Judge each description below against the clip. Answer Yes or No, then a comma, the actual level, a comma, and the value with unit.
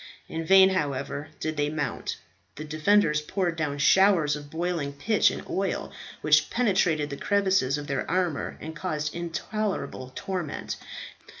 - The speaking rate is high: No, average, 140 wpm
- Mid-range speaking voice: Yes, medium, 155 Hz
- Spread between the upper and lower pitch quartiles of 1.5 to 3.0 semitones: No, average, 4.4 semitones